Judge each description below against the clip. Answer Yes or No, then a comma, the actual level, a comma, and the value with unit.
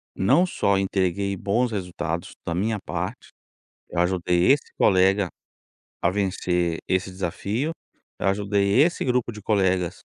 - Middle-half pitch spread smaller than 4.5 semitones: Yes, average, 2.7 semitones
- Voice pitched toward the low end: Yes, very low, 95 Hz